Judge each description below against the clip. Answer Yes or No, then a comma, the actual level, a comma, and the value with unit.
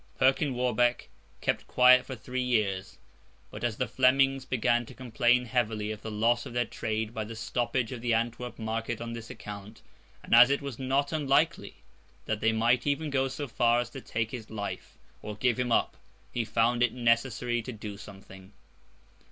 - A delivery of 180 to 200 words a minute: Yes, average, 185 wpm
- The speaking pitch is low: Yes, low, 120 Hz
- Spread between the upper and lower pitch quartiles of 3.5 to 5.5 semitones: No, narrow, 2.4 semitones